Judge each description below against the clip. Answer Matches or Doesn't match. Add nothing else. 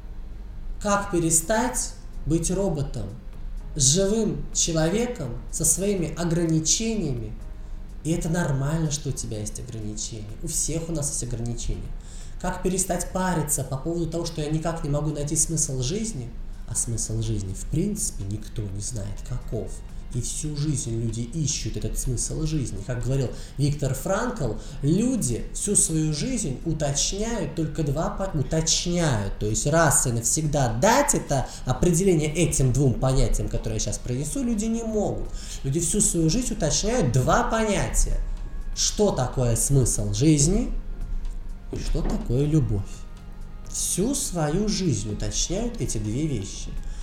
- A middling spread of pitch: Doesn't match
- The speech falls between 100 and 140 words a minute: Matches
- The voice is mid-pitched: Matches